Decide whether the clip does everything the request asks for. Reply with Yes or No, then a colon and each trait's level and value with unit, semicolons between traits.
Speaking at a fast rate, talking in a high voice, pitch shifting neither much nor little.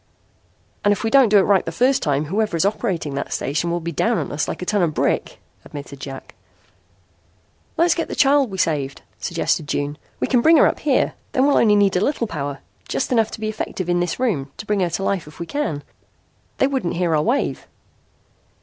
No: fast, 220 wpm; high, 195 Hz; wide, 7.3 semitones